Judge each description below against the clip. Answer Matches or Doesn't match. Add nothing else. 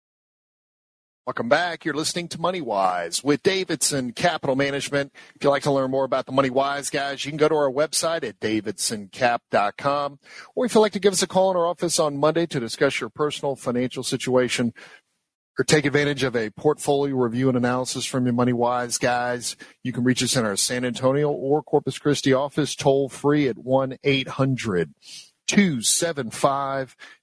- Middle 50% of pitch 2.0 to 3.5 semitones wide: Matches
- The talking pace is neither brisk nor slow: Matches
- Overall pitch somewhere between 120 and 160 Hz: Matches